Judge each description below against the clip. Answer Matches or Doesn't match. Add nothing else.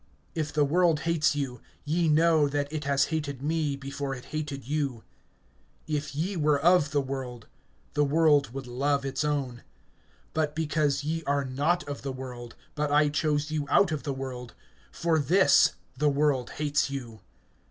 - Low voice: Doesn't match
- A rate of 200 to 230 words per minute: Doesn't match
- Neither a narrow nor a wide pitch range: Doesn't match